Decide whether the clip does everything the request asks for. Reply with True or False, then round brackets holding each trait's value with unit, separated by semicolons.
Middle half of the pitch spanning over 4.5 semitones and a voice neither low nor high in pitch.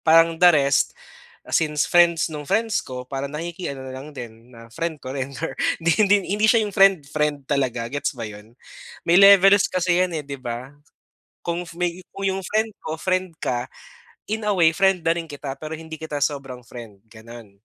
True (5.2 semitones; 155 Hz)